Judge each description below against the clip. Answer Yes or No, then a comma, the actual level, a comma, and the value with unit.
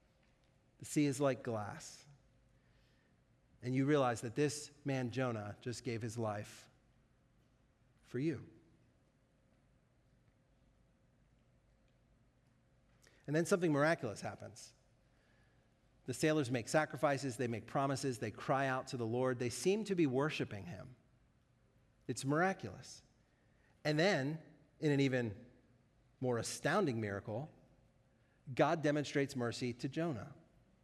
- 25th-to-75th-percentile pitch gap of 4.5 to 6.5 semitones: No, average, 2.7 semitones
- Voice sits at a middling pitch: No, low, 130 Hz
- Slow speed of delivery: Yes, slow, 110 wpm